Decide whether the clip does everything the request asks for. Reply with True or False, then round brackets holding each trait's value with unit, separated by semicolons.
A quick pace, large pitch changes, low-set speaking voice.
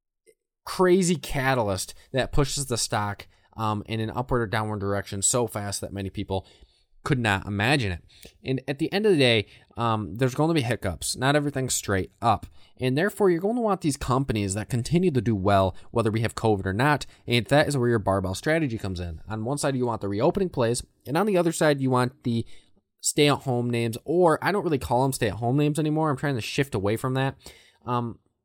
True (225 wpm; 6.0 semitones; 120 Hz)